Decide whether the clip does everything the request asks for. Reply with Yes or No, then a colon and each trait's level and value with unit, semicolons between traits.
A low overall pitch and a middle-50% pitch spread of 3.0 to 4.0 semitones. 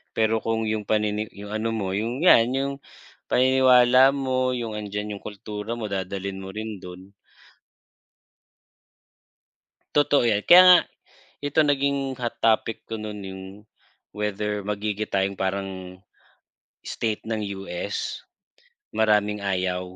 Yes: low, 110 Hz; average, 3.5 semitones